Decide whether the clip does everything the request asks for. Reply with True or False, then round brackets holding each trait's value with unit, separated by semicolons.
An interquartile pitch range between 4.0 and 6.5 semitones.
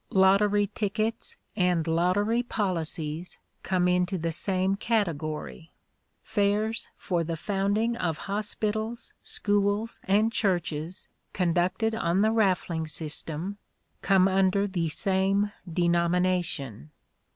False (3.3 semitones)